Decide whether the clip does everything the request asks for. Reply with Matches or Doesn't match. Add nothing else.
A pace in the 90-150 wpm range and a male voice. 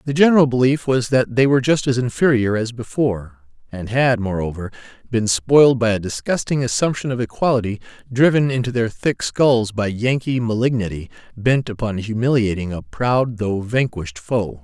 Doesn't match